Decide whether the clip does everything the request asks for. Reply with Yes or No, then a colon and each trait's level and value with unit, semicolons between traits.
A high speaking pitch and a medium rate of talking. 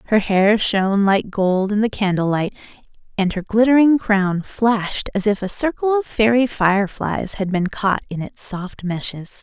Yes: high, 205 Hz; average, 170 wpm